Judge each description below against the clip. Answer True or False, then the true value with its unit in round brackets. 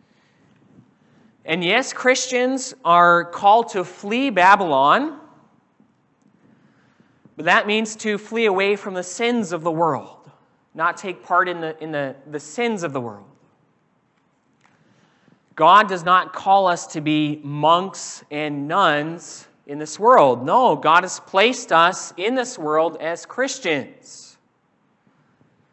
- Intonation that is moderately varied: False (5.7 semitones)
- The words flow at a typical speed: False (130 wpm)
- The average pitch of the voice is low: False (180 Hz)